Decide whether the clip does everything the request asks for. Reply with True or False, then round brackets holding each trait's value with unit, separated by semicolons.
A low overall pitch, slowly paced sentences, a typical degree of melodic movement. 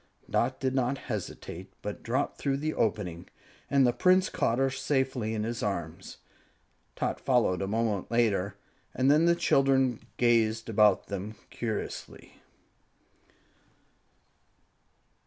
True (115 Hz; 120 wpm; 4.2 semitones)